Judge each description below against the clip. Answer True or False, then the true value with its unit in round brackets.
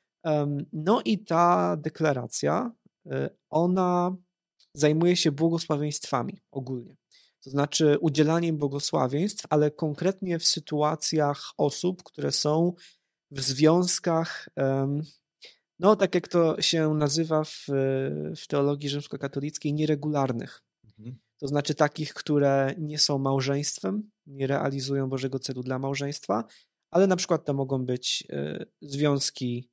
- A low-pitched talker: False (150 Hz)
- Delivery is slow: True (105 wpm)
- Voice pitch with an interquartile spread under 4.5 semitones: True (3.2 semitones)